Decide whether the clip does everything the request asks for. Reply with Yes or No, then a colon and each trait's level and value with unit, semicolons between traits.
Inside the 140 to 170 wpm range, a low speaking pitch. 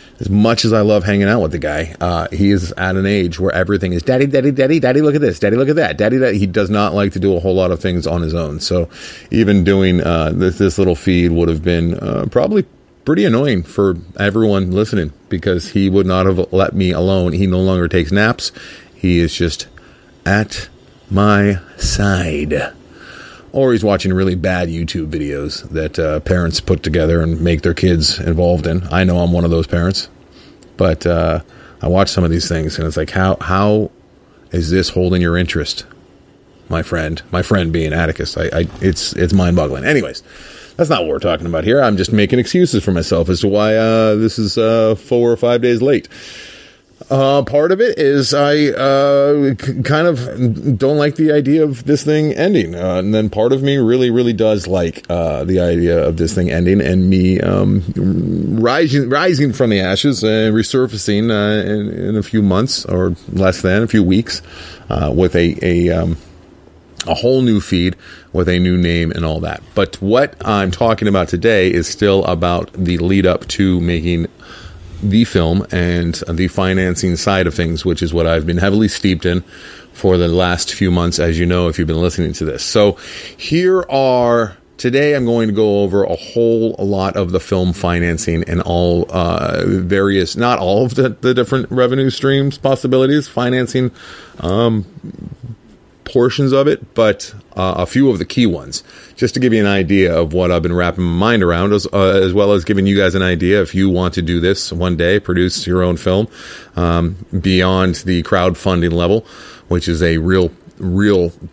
No: average, 200 wpm; very low, 95 Hz